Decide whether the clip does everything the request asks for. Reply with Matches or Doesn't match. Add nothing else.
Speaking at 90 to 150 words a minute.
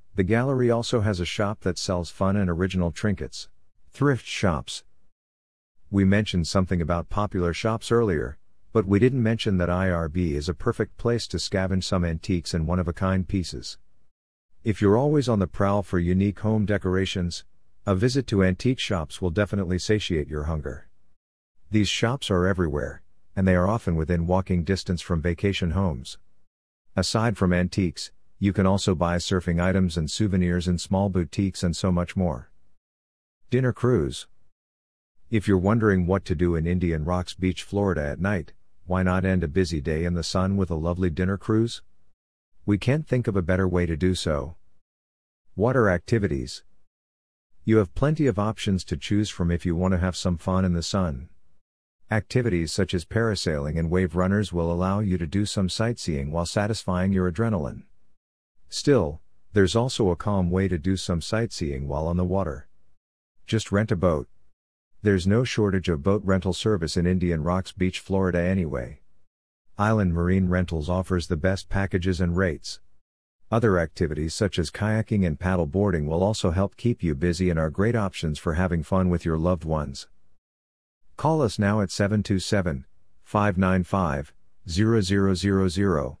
Doesn't match